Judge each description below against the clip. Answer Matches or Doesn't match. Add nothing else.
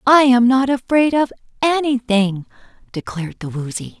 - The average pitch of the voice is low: Doesn't match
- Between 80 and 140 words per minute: Matches